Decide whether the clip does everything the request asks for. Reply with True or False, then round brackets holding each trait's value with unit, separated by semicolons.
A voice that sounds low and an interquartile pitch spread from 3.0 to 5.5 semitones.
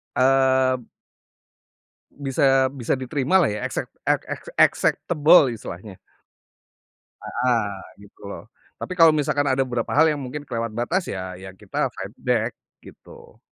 True (130 Hz; 3.8 semitones)